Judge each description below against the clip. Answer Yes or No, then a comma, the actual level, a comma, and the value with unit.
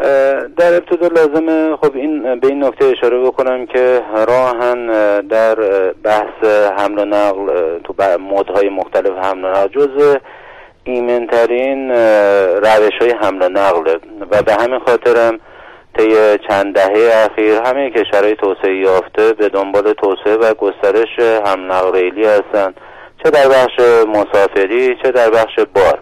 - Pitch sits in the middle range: No, low, 110 Hz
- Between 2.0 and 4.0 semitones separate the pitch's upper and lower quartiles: No, average, 4.6 semitones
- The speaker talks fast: No, average, 140 wpm